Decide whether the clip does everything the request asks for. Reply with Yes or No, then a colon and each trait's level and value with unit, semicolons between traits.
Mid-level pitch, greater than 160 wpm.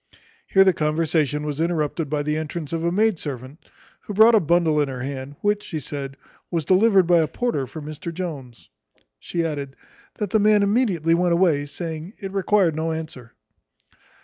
Yes: medium, 165 Hz; average, 180 wpm